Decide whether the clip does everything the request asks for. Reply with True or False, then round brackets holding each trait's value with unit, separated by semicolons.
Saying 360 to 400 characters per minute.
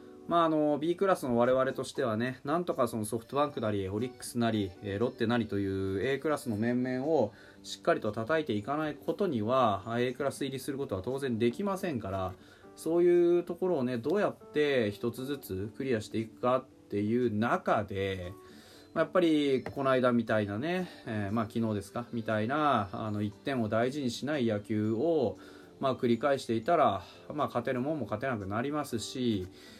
True (370 characters per minute)